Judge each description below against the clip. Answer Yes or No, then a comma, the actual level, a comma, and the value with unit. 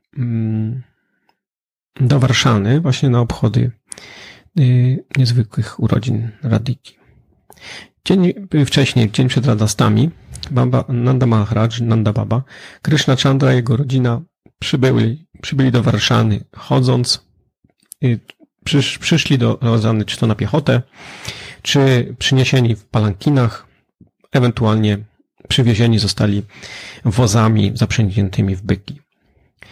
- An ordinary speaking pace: No, slow, 100 wpm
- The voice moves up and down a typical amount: Yes, average, 3.1 semitones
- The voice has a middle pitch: No, low, 120 Hz